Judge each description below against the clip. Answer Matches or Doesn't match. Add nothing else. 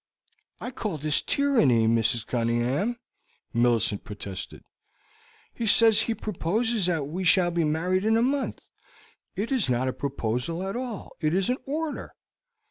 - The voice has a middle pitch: Matches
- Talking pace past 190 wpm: Doesn't match